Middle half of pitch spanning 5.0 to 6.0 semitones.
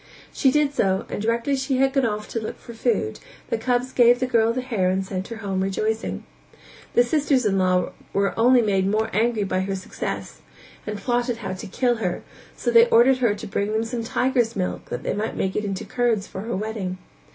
No: average, 3.7 semitones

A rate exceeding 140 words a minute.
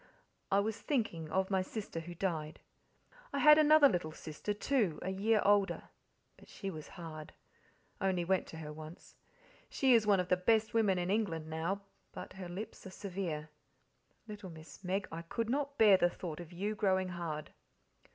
Yes: average, 180 wpm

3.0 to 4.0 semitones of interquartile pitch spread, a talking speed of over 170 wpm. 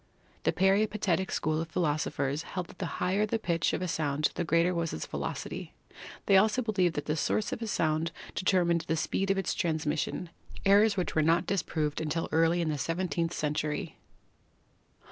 Yes: average, 3.4 semitones; average, 180 wpm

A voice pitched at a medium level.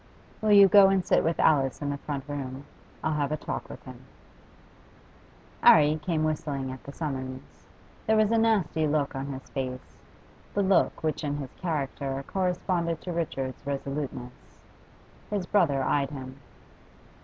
Yes: medium, 150 Hz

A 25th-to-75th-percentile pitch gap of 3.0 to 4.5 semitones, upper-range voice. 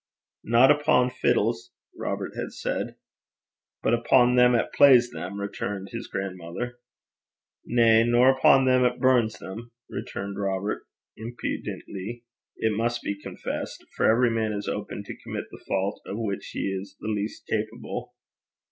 No: average, 3.4 semitones; low, 115 Hz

